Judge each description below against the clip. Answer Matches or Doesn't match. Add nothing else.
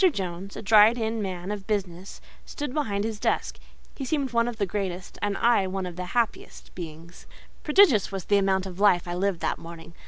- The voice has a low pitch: Doesn't match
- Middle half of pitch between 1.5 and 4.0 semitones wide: Matches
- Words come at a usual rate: Doesn't match